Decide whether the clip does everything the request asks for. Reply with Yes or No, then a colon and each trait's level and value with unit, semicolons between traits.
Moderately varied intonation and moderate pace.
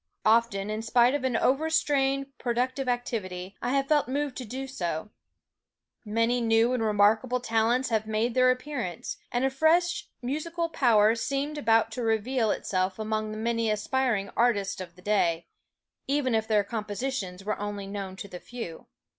Yes: average, 3.9 semitones; average, 165 wpm